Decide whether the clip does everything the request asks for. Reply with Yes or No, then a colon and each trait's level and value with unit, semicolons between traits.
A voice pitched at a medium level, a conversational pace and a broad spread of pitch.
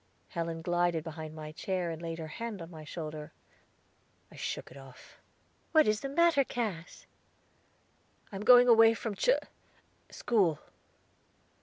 Yes: medium, 175 Hz; average, 145 wpm; wide, 6.0 semitones